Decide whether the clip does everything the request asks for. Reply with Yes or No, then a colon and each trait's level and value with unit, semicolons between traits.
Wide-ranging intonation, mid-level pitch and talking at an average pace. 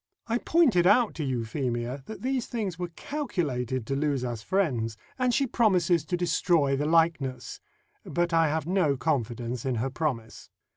Yes: wide, 6.4 semitones; medium, 155 Hz; average, 160 wpm